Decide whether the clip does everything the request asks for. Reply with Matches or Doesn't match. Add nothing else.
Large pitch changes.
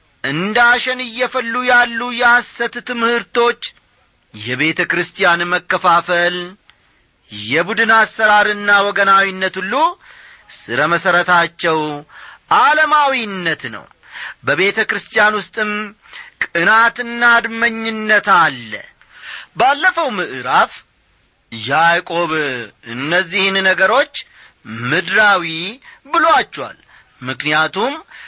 Matches